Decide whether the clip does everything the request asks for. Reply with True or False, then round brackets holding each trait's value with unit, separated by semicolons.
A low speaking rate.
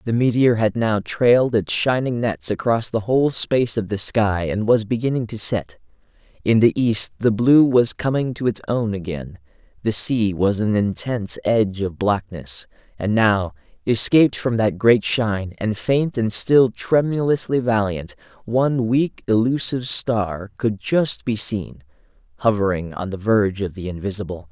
False (165 wpm)